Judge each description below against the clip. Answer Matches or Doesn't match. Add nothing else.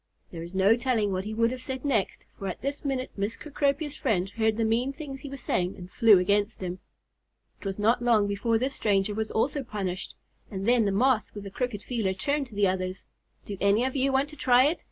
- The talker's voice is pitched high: Matches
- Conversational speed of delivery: Doesn't match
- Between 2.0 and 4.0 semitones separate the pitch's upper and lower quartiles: Doesn't match